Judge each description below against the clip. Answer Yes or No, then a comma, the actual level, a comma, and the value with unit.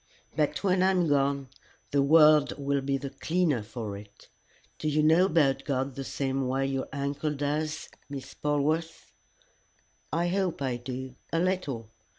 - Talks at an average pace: Yes, average, 160 wpm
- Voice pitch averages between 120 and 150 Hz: Yes, medium, 140 Hz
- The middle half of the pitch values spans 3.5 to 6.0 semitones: No, average, 2.9 semitones